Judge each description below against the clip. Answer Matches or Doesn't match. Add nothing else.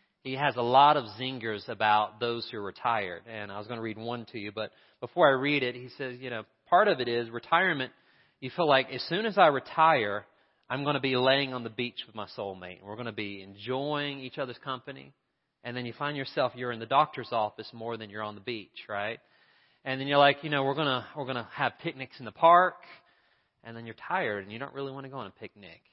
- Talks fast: Matches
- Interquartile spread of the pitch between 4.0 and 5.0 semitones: Doesn't match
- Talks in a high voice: Doesn't match